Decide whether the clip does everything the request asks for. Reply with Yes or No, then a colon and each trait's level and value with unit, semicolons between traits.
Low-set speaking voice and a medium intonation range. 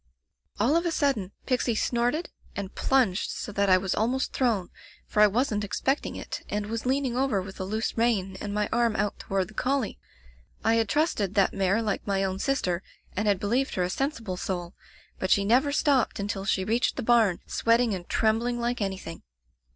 No: high, 215 Hz; average, 3.9 semitones